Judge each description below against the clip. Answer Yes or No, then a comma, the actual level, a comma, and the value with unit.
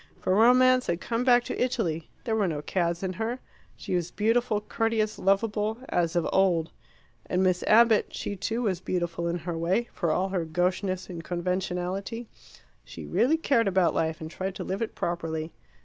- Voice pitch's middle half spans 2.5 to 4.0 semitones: No, average, 4.5 semitones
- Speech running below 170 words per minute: No, average, 180 wpm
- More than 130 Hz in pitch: Yes, high, 190 Hz